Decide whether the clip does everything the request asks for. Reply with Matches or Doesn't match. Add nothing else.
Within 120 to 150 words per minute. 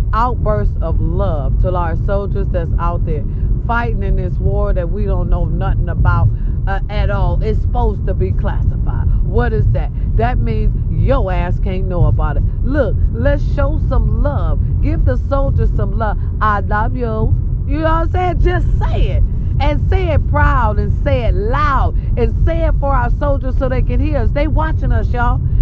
Doesn't match